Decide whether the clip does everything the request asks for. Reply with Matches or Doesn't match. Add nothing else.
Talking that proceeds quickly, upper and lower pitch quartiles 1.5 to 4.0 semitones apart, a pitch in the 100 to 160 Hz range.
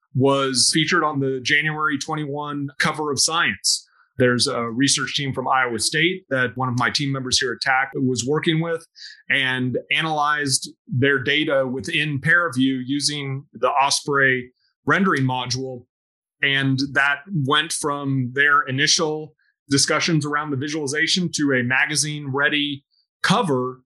Doesn't match